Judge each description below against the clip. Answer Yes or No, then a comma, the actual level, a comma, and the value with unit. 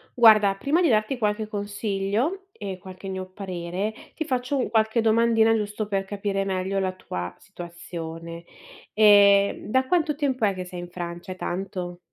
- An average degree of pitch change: Yes, average, 3.2 semitones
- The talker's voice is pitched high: Yes, high, 200 Hz